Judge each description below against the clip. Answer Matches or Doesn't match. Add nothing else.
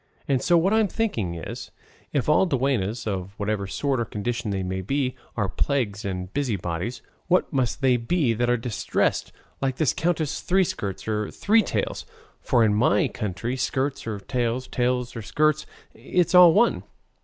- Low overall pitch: Matches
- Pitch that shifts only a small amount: Doesn't match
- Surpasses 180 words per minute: Doesn't match